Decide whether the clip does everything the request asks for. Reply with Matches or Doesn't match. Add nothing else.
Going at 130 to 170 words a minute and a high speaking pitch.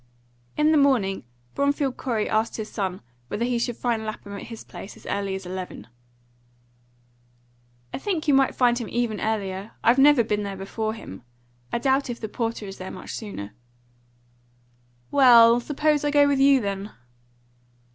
Matches